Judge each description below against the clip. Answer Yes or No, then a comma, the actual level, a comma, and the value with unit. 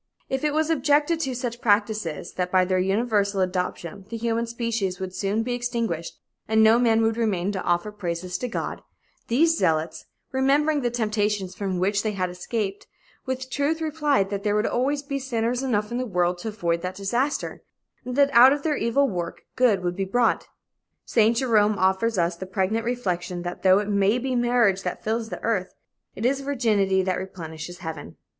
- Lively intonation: No, average, 4.7 semitones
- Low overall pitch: No, high, 215 Hz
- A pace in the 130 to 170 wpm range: No, average, 190 wpm